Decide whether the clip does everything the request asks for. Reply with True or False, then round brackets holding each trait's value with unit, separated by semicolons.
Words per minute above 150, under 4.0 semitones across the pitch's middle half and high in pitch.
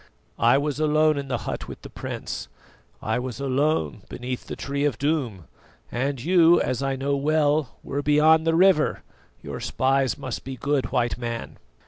False (170 wpm; 3.1 semitones; 140 Hz)